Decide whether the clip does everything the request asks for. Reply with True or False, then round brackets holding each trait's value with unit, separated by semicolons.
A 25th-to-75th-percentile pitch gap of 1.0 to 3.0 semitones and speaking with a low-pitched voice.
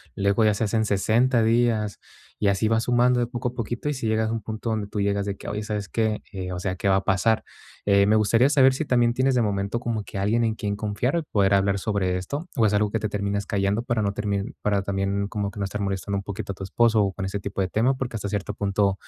True (2.7 semitones; 105 Hz)